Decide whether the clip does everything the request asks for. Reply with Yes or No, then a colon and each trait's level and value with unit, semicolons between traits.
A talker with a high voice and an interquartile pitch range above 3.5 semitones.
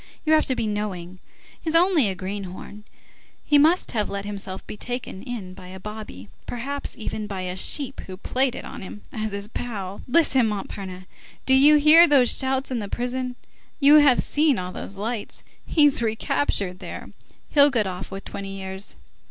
Yes: high, 215 Hz; wide, 5.6 semitones